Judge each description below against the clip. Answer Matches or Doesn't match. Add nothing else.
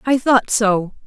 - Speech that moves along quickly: Doesn't match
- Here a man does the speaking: Doesn't match